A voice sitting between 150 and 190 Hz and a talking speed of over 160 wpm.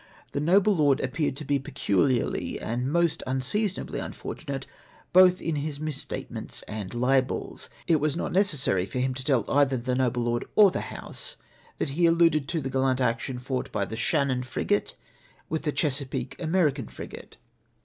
No: low, 135 Hz; average, 170 wpm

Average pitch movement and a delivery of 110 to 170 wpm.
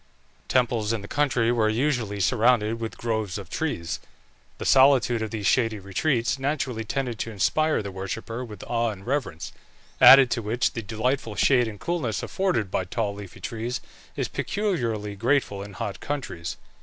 Yes: average, 3.6 semitones; average, 165 wpm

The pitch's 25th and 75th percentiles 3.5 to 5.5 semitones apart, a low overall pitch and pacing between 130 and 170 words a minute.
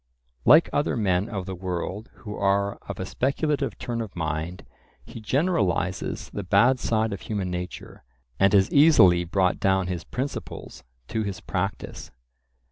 Yes: average, 4.2 semitones; low, 100 Hz; average, 150 wpm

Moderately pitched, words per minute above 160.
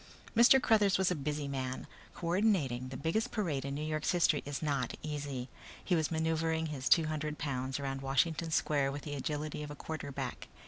Yes: medium, 150 Hz; average, 190 wpm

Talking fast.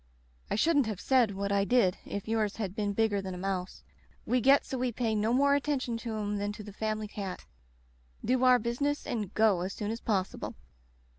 Yes: fast, 210 wpm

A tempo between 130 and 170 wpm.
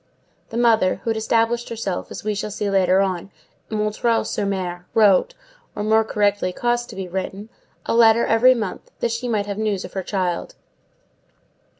No: average, 185 wpm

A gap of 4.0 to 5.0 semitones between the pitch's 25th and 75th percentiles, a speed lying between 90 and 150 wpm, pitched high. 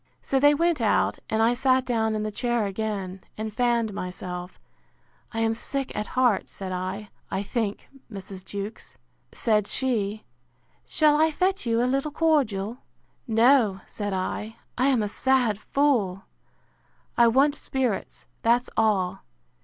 Yes: average, 4.4 semitones; average, 145 wpm; high, 225 Hz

